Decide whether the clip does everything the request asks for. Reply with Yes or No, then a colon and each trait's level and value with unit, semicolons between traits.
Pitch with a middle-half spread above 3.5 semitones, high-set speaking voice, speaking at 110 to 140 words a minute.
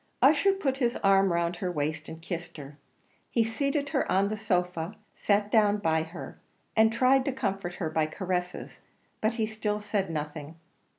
No: average, 4.7 semitones; high, 195 Hz; average, 175 wpm